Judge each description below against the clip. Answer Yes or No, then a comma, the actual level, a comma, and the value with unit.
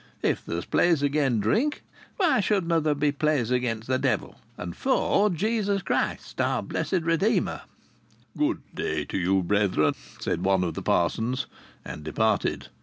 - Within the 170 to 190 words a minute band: No, average, 150 wpm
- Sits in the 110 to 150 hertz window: Yes, medium, 140 Hz